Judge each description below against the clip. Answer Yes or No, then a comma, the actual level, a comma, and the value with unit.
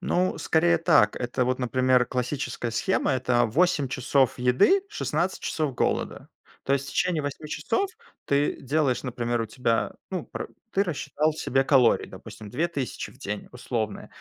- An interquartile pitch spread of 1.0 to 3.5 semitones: No, average, 4.3 semitones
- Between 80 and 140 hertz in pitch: Yes, low, 135 Hz